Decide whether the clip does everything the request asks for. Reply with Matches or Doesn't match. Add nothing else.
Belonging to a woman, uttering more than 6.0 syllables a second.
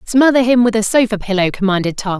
Matches